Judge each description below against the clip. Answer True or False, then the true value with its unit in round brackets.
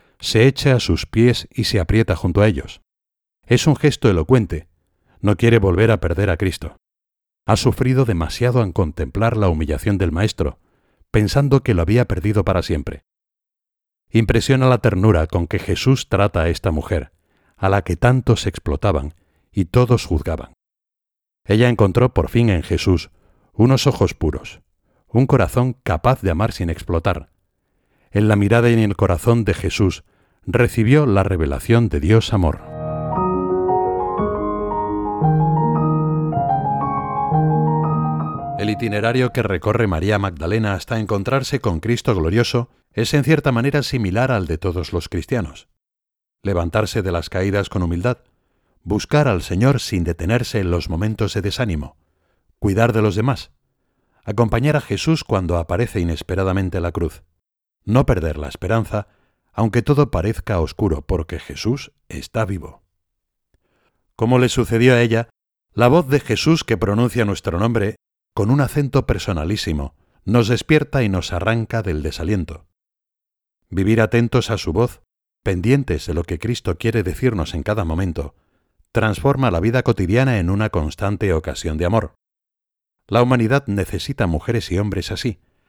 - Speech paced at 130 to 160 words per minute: True (145 wpm)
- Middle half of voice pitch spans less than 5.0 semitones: False (5.4 semitones)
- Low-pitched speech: True (100 Hz)